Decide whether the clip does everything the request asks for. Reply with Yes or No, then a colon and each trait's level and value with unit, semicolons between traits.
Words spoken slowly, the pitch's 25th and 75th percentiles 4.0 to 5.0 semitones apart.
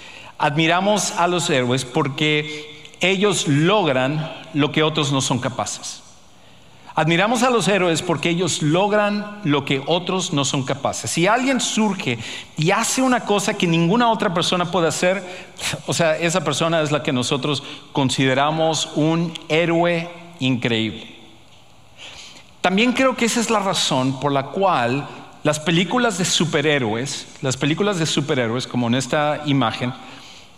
No: average, 145 wpm; average, 4.7 semitones